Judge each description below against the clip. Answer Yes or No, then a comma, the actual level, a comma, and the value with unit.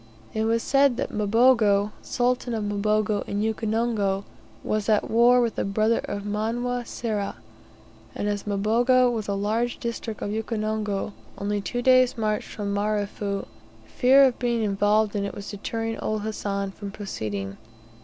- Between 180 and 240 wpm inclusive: No, average, 155 wpm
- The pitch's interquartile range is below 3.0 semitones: Yes, narrow, 2.5 semitones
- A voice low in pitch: No, high, 215 Hz